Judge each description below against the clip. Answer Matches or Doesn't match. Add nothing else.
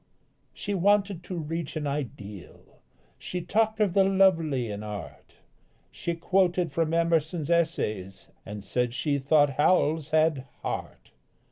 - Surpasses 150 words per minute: Doesn't match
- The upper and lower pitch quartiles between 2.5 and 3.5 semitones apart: Doesn't match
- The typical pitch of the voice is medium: Matches